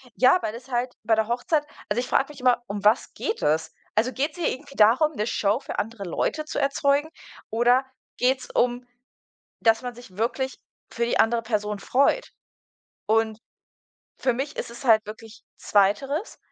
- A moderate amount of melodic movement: Yes, average, 3.6 semitones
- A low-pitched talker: No, high, 240 Hz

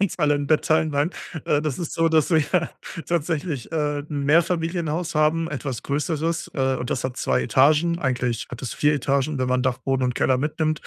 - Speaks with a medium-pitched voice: Yes, medium, 150 Hz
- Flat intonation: No, average, 3.4 semitones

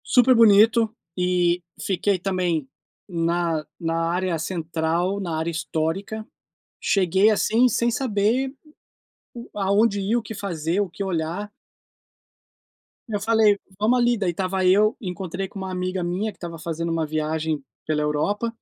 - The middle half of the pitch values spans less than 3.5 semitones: No, average, 3.9 semitones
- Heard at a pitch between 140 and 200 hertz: Yes, medium, 185 Hz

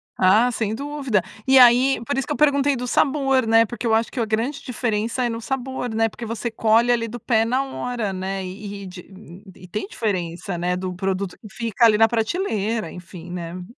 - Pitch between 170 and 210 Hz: No, high, 225 Hz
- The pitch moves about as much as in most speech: Yes, average, 4.2 semitones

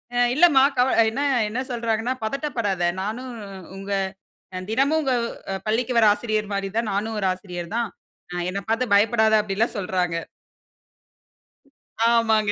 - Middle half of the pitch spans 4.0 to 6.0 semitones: No, average, 3.3 semitones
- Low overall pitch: No, high, 220 Hz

